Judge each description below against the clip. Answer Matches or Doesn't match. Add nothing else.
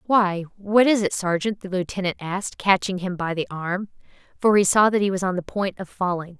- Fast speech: Matches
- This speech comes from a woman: Matches